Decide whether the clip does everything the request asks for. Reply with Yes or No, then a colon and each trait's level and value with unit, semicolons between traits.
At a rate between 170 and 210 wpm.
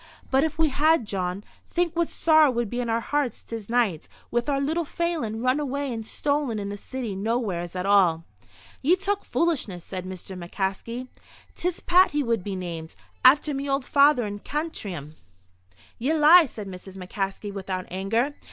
Yes: average, 175 wpm